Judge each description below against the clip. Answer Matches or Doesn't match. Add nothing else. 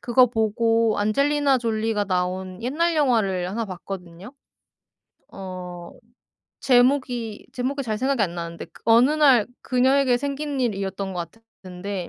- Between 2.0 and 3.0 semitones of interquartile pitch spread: Doesn't match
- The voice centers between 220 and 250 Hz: Matches